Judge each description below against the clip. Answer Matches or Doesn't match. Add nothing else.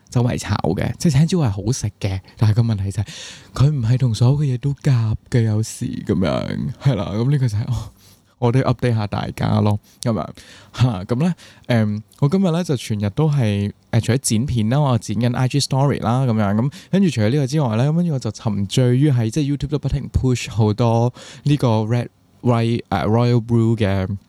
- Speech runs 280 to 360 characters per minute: Doesn't match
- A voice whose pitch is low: Matches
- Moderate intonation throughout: Matches